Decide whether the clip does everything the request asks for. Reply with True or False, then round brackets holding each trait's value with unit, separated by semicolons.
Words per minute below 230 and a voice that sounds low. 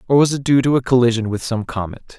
False (275 wpm; 125 Hz)